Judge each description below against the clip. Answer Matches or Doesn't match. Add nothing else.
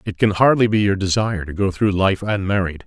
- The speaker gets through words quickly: Matches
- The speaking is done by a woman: Doesn't match